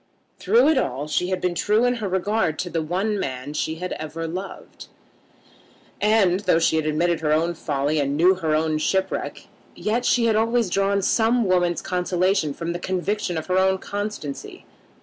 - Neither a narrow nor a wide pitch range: Yes, average, 4.3 semitones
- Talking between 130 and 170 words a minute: No, average, 180 wpm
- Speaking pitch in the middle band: Yes, medium, 180 Hz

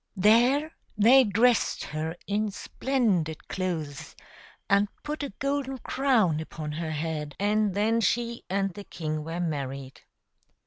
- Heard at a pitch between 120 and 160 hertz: No, high, 200 Hz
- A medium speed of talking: No, slow, 130 wpm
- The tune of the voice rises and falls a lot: Yes, wide, 7.0 semitones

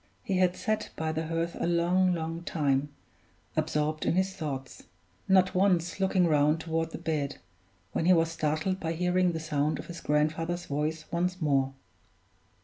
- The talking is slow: No, average, 165 wpm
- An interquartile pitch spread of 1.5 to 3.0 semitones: Yes, average, 2.7 semitones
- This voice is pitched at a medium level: Yes, medium, 165 Hz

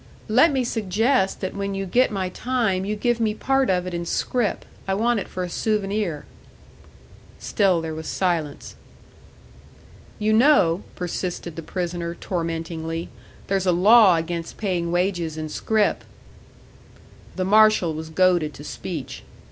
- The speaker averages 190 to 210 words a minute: No, average, 145 wpm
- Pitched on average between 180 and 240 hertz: Yes, medium, 185 Hz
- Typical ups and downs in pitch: Yes, average, 4.1 semitones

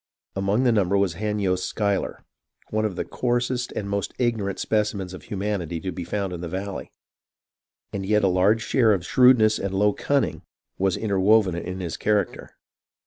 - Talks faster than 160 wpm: Yes, average, 175 wpm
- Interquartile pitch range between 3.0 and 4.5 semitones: No, narrow, 2.5 semitones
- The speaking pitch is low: Yes, low, 100 Hz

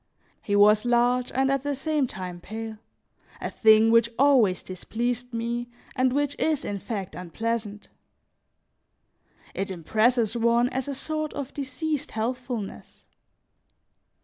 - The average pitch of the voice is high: Yes, high, 235 Hz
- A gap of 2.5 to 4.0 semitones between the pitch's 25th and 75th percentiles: Yes, average, 3.4 semitones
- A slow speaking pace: Yes, slow, 125 wpm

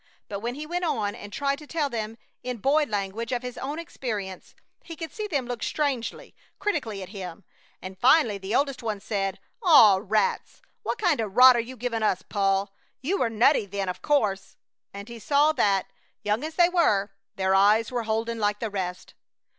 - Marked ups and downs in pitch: Yes, wide, 5.9 semitones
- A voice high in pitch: Yes, high, 230 Hz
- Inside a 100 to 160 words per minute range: No, average, 195 wpm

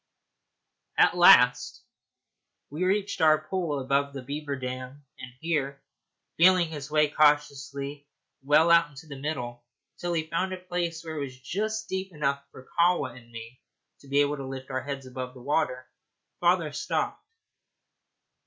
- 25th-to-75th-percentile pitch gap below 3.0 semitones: No, average, 3.8 semitones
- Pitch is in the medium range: Yes, medium, 145 Hz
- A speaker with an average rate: Yes, average, 155 wpm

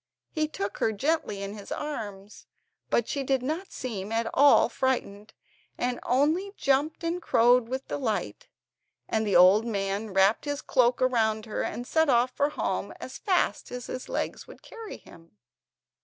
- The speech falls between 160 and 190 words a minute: Yes, average, 165 wpm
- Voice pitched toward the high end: Yes, high, 245 Hz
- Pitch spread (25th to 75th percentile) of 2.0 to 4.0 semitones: No, average, 5.3 semitones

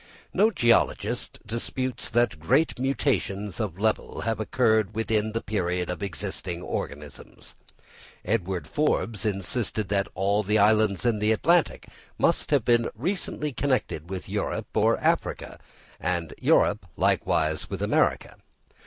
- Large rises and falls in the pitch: No, average, 3.8 semitones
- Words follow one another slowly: Yes, slow, 125 wpm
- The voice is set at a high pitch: No, low, 110 Hz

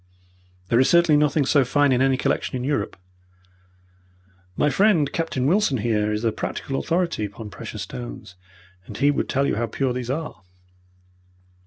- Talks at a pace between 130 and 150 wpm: No, average, 165 wpm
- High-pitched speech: No, low, 135 Hz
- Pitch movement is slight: No, average, 4.3 semitones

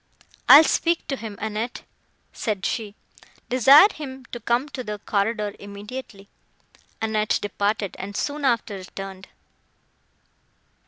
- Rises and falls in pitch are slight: No, average, 4.3 semitones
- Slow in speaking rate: Yes, slow, 120 wpm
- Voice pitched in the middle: No, high, 220 Hz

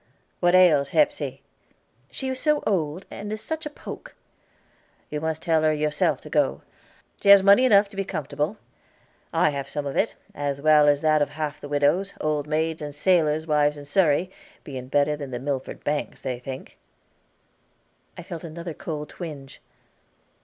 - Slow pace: No, average, 175 wpm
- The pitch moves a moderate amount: Yes, average, 4.1 semitones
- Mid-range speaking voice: Yes, medium, 155 Hz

